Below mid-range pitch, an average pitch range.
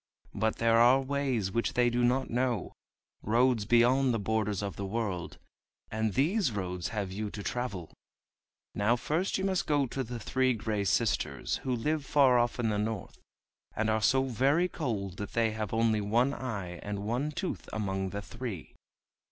Yes: low, 115 Hz; average, 4.0 semitones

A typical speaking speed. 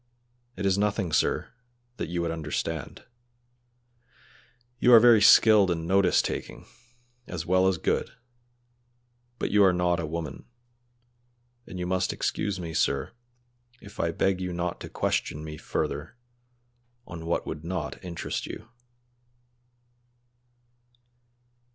No: slow, 125 wpm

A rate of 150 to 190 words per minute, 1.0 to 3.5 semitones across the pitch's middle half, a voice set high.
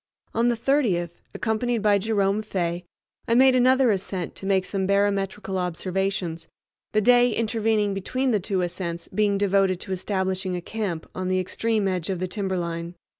Yes: average, 165 wpm; average, 3.0 semitones; high, 195 Hz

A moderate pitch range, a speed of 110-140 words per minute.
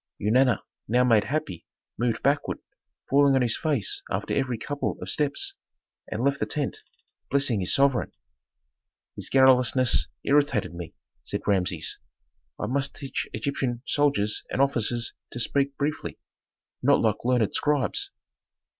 Yes: average, 3.7 semitones; slow, 135 wpm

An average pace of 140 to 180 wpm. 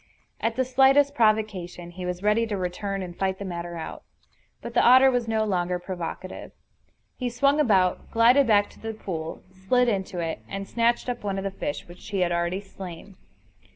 No: average, 190 wpm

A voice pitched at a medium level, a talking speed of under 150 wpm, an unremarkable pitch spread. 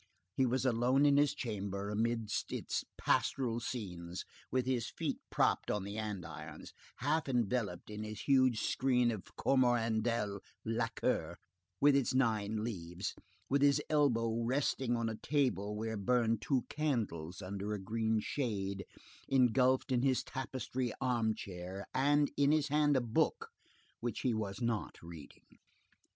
No: low, 115 Hz; average, 140 wpm; average, 3.9 semitones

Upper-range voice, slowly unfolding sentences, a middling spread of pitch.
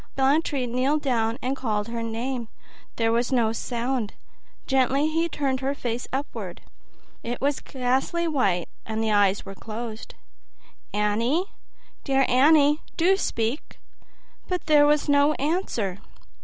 Yes: very high, 255 Hz; slow, 130 wpm; average, 4.2 semitones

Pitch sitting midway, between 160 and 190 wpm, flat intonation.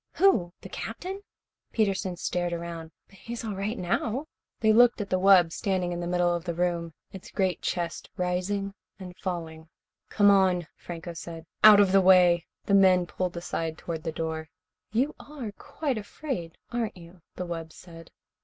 No: medium, 180 Hz; average, 170 wpm; average, 3.0 semitones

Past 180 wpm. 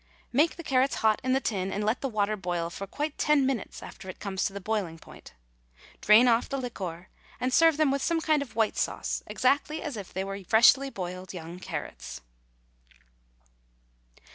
Yes: average, 190 wpm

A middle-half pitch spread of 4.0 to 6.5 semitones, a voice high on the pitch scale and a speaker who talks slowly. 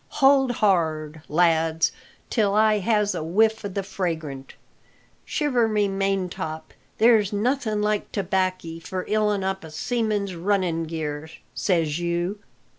Yes: average, 4.4 semitones; high, 195 Hz; slow, 125 wpm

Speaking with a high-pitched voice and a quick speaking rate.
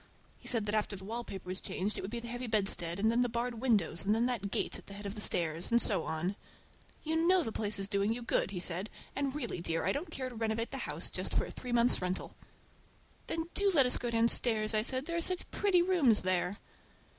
Yes: high, 225 Hz; fast, 250 wpm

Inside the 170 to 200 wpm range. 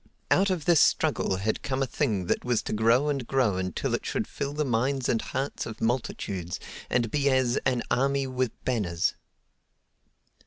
Yes: average, 180 wpm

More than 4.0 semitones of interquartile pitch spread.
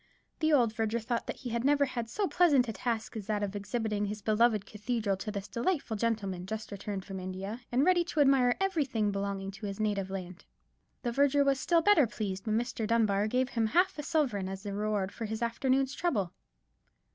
Yes: average, 4.5 semitones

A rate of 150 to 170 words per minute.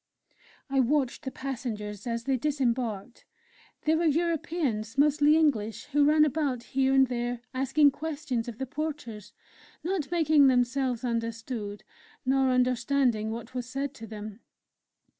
No: slow, 135 wpm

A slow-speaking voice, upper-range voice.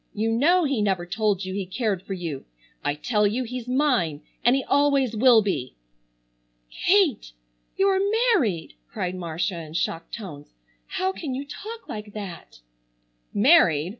No: average, 150 wpm; high, 210 Hz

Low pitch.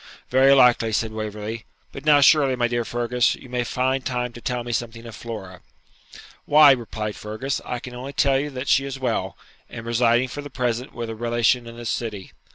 Yes: low, 120 Hz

